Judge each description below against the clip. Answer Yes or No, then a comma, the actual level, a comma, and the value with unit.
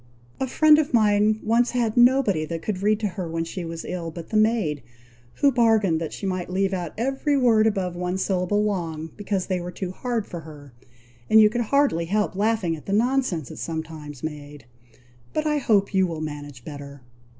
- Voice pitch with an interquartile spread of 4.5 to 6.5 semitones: Yes, average, 5.3 semitones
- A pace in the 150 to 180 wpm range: No, average, 200 wpm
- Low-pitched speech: No, high, 190 Hz